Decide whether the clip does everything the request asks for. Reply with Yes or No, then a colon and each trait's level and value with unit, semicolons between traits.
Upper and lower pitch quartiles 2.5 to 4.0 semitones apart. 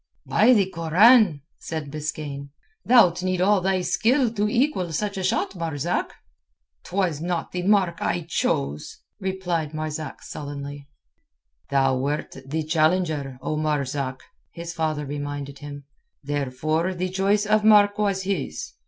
No: average, 4.7 semitones